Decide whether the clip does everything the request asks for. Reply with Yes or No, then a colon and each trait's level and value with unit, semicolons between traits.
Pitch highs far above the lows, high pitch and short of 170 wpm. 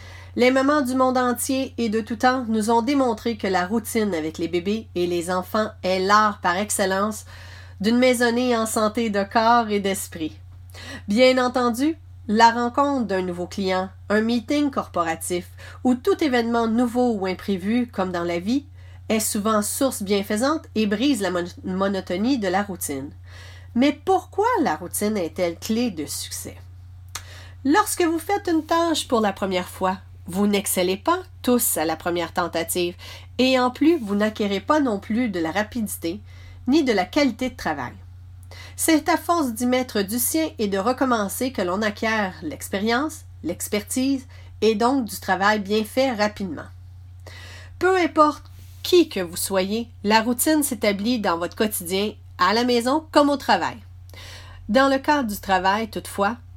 Yes: wide, 6.3 semitones; high, 210 Hz; average, 160 wpm